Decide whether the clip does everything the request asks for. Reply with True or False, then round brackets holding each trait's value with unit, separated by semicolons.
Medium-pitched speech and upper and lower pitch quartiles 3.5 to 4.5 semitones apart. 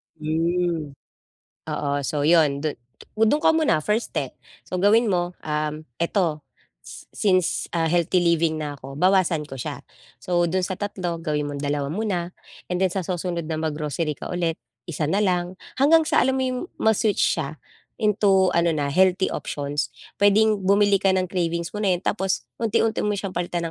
True (175 Hz; 4.0 semitones)